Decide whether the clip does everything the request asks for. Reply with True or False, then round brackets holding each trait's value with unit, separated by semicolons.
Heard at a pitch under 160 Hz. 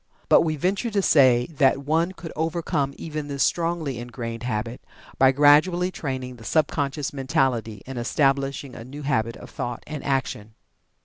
True (140 Hz)